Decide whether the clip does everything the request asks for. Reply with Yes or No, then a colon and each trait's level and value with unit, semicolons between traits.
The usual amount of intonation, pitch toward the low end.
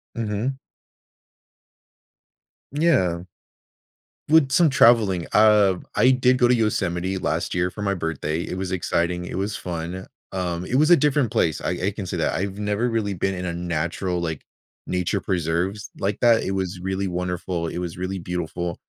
Yes: average, 3.4 semitones; very low, 95 Hz